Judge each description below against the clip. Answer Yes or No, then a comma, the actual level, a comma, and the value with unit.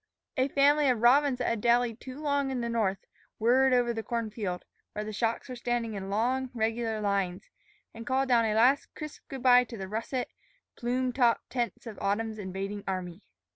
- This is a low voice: No, high, 235 Hz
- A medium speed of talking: Yes, average, 195 wpm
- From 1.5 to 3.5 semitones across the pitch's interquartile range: Yes, average, 3.2 semitones